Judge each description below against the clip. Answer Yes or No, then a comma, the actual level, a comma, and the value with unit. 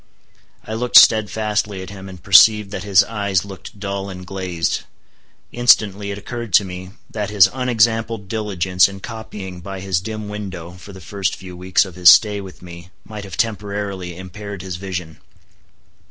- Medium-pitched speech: No, low, 100 Hz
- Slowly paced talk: No, average, 170 wpm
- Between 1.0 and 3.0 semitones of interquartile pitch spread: Yes, narrow, 2.4 semitones